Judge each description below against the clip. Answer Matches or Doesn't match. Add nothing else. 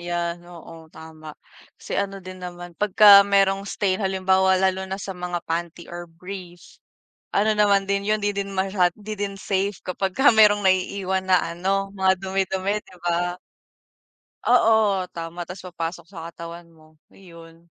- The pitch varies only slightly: Matches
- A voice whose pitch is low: Doesn't match